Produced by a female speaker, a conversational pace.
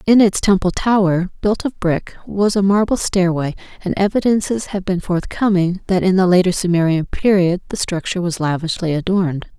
Yes: female; average, 170 wpm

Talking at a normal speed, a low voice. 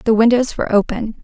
No: average, 195 wpm; high, 225 Hz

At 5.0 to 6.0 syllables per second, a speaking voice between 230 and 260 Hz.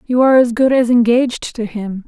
Yes: 5.6 syllables/s; high, 240 Hz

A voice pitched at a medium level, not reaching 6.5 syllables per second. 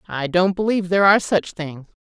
Yes: medium, 180 Hz; 6.3 syllables/s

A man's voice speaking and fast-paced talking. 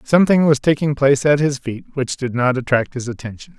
Yes: male; fast, 220 wpm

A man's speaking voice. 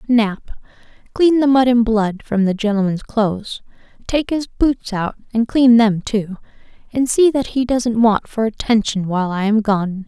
No: female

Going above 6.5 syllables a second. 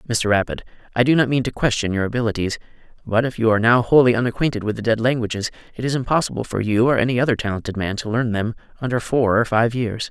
Yes: 6.8 syllables/s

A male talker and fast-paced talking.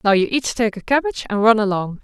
No: female; fast, 265 wpm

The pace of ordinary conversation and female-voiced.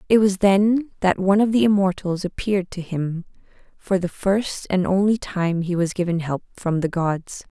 Yes: average, 190 wpm; female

